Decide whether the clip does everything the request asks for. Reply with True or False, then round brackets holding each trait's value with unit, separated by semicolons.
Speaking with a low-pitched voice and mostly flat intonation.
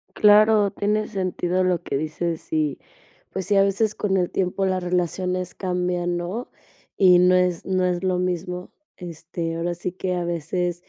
False (180 Hz; 1.5 semitones)